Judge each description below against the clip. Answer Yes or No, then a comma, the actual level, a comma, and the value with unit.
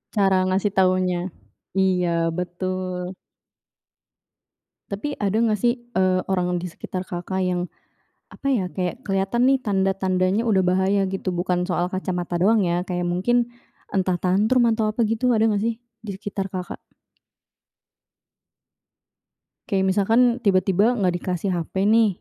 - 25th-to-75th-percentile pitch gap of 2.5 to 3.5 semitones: Yes, average, 2.8 semitones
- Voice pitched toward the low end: No, high, 190 Hz